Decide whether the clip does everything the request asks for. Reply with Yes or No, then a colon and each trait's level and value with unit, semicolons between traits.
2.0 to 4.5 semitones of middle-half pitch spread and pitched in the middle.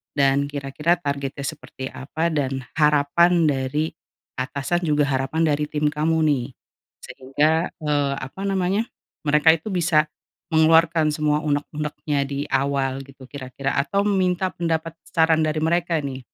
Yes: average, 2.7 semitones; medium, 150 Hz